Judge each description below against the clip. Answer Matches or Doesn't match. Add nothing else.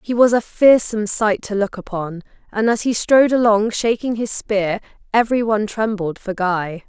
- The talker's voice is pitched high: Matches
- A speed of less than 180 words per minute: Doesn't match